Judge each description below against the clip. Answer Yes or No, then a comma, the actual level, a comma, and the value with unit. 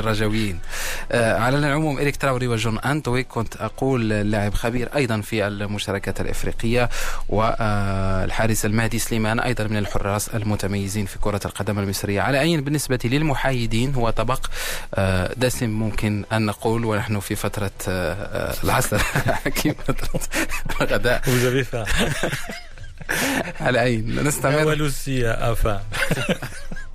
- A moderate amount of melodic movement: Yes, average, 3.3 semitones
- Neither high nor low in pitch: No, low, 110 Hz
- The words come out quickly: No, average, 105 wpm